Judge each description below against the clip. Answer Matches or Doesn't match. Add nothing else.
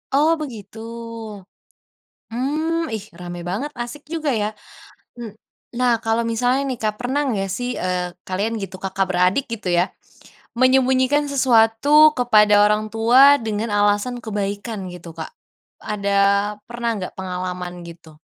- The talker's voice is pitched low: Doesn't match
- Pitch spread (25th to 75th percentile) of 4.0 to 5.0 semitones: Matches